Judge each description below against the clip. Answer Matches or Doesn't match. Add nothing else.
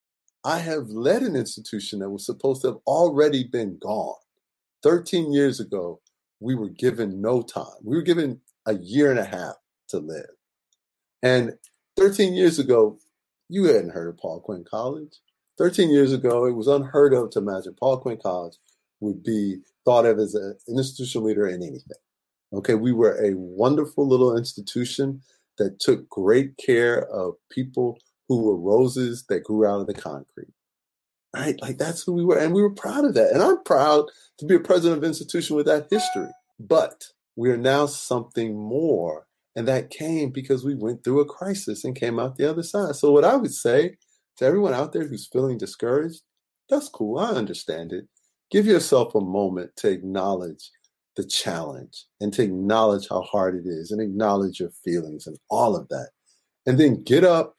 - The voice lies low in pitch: Matches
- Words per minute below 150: Doesn't match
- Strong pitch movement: Matches